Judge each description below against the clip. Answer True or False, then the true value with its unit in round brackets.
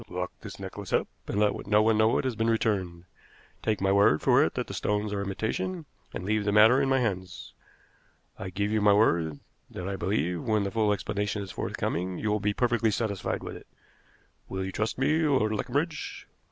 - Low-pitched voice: True (105 Hz)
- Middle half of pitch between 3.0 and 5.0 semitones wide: False (2.6 semitones)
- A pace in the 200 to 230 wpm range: True (205 wpm)